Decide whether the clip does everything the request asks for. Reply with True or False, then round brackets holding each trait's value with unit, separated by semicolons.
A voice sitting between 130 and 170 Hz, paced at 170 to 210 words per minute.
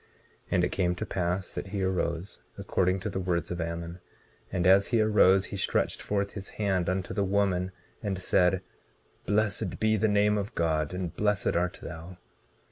False (95 Hz; 185 wpm)